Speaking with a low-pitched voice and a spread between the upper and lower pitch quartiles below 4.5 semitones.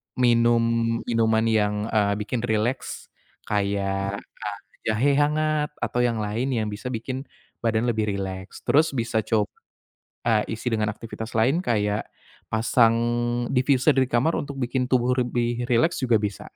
Yes: low, 115 Hz; average, 2.7 semitones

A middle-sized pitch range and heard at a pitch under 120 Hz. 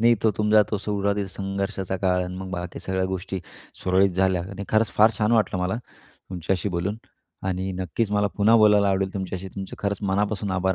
No: narrow, 1.8 semitones; very low, 95 Hz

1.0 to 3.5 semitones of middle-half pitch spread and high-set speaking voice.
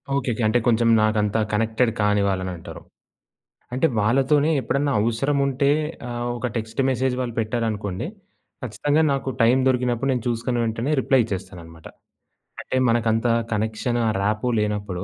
No: average, 3.1 semitones; low, 115 Hz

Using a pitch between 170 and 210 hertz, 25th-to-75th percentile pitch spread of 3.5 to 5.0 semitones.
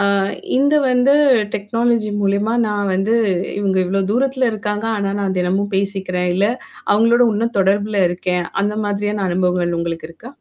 No: high, 200 Hz; average, 2.7 semitones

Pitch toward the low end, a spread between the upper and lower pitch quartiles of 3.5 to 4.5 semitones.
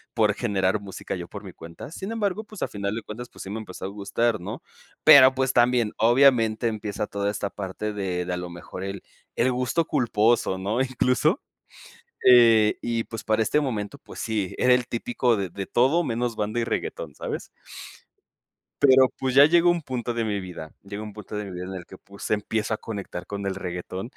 Yes: low, 110 Hz; average, 4.0 semitones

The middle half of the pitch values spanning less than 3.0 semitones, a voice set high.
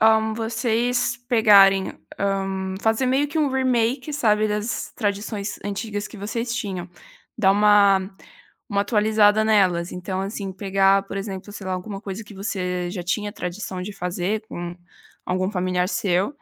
Yes: narrow, 2.5 semitones; high, 205 Hz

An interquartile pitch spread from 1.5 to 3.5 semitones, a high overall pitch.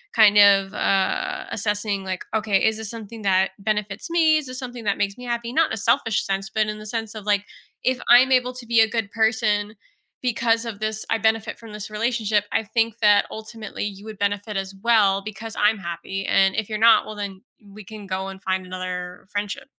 Yes: narrow, 2.4 semitones; high, 215 Hz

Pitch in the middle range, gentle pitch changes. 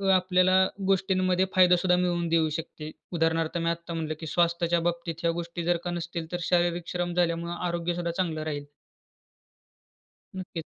Yes: medium, 170 Hz; narrow, 1.2 semitones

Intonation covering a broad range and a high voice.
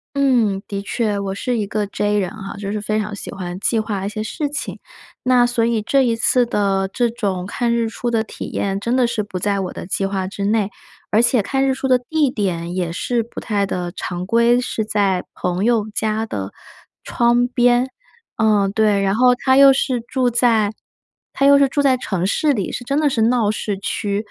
No: average, 3.5 semitones; high, 220 Hz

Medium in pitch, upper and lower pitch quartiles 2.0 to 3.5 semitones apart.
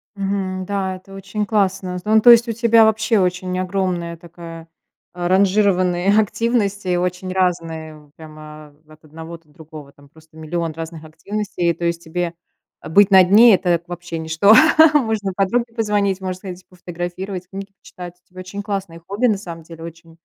Yes: medium, 180 Hz; average, 3.1 semitones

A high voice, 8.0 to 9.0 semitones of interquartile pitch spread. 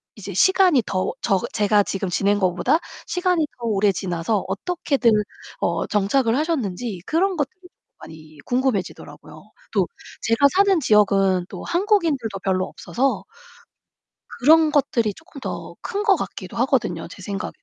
Yes: high, 230 Hz; wide, 8.4 semitones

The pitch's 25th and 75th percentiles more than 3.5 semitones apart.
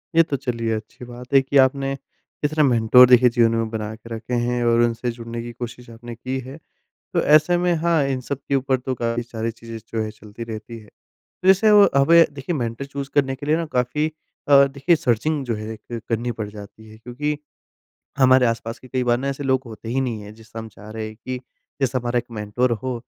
No: average, 3.1 semitones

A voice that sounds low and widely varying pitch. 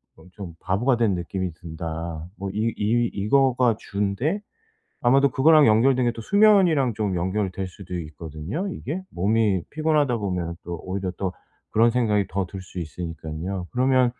Yes: low, 100 Hz; wide, 5.8 semitones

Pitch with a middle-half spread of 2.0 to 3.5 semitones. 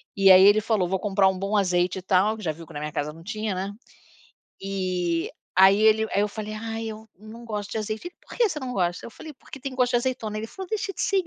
Yes: average, 3.1 semitones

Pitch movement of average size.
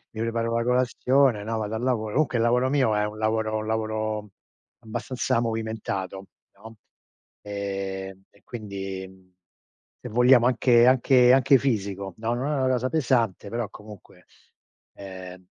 Yes: average, 3.3 semitones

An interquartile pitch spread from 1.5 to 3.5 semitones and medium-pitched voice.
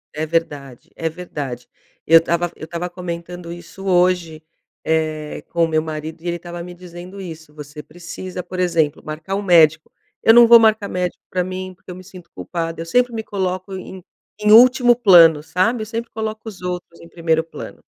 Yes: narrow, 2.5 semitones; medium, 175 Hz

